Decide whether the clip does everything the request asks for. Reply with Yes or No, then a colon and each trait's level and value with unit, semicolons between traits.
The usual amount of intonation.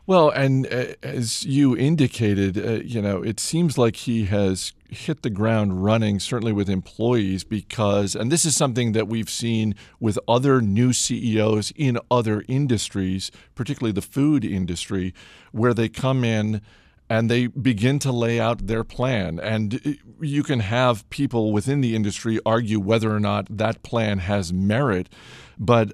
Yes: average, 3.2 semitones